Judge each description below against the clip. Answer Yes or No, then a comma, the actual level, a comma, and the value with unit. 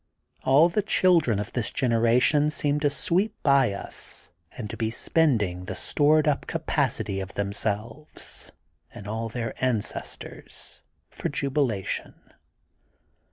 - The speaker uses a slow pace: Yes, slow, 125 wpm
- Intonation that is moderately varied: No, wide, 5.7 semitones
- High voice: No, low, 125 Hz